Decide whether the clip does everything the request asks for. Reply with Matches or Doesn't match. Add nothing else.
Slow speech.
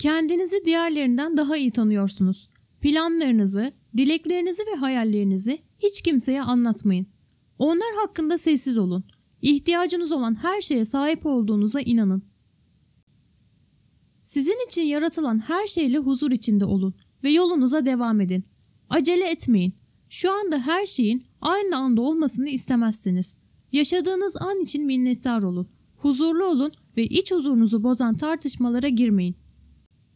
Doesn't match